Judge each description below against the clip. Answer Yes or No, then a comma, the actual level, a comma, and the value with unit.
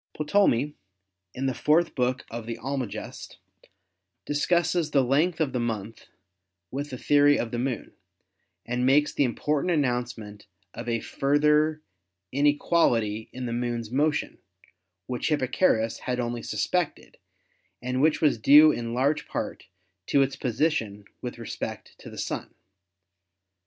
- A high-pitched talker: No, low, 130 Hz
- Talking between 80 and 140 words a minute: Yes, slow, 135 wpm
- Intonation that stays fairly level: No, average, 3.9 semitones